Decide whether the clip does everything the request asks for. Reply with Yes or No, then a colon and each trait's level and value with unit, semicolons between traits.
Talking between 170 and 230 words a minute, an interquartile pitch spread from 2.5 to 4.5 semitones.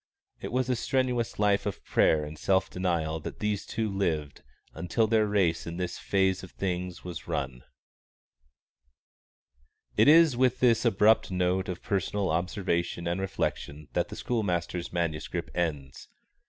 No: average, 145 wpm; average, 3.7 semitones